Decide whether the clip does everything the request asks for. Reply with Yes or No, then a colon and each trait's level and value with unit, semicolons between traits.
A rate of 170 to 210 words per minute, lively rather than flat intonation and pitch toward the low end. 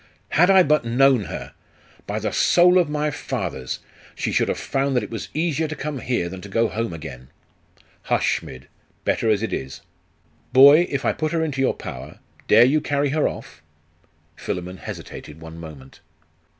Yes: average, 180 wpm; wide, 8.6 semitones; low, 130 Hz